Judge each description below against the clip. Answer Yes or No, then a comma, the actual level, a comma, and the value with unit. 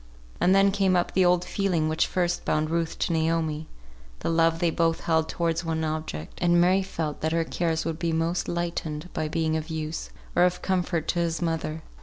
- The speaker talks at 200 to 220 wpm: Yes, fast, 205 wpm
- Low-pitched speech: No, medium, 165 Hz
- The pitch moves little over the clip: Yes, narrow, 1.6 semitones